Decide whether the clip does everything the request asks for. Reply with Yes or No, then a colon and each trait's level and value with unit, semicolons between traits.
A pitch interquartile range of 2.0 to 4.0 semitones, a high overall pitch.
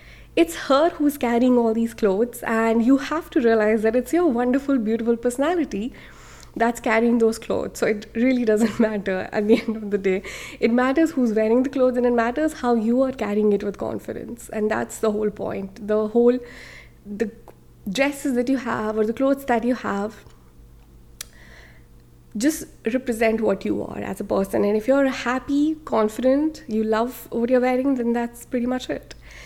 Yes: average, 3.1 semitones; high, 235 Hz